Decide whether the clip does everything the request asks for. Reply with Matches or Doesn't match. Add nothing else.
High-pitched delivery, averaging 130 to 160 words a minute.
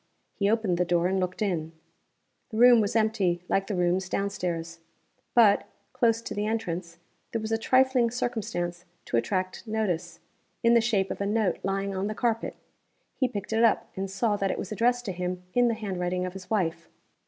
Doesn't match